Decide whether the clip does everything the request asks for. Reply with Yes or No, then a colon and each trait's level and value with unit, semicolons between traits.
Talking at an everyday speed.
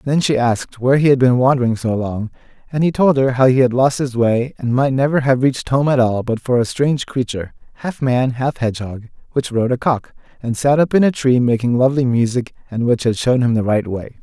No: fast, 245 wpm